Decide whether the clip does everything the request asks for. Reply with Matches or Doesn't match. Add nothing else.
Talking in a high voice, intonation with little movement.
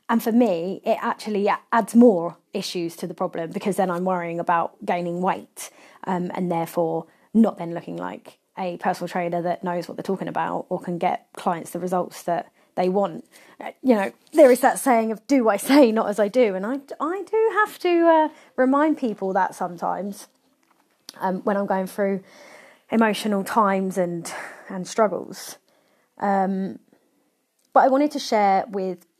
Doesn't match